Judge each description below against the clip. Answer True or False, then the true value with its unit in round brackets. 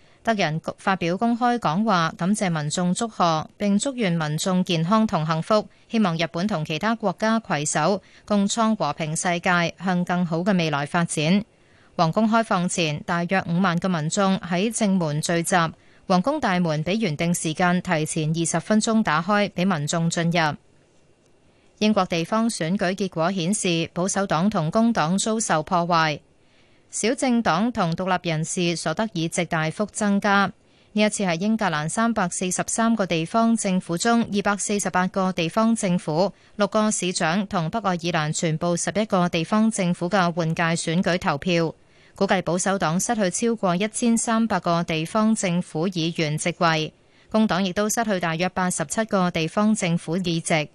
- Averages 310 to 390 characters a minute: False (255 characters per minute)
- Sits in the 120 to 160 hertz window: False (180 Hz)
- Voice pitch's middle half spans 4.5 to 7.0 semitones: False (3.8 semitones)